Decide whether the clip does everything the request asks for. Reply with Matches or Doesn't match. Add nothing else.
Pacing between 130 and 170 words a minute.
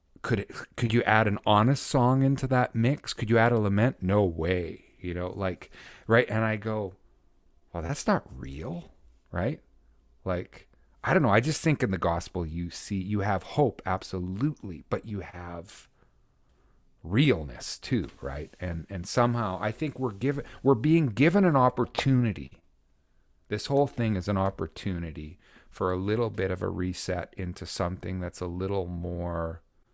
Matches